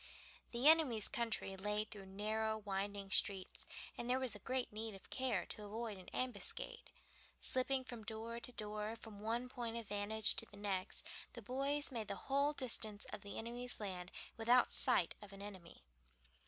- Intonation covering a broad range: No, average, 3.4 semitones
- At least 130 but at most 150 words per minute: No, average, 170 wpm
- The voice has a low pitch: No, high, 220 Hz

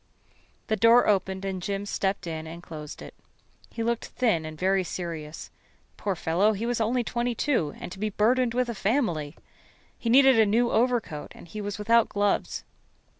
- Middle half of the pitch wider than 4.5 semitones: Yes, average, 5.0 semitones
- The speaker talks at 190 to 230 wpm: No, average, 180 wpm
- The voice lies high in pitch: Yes, high, 205 Hz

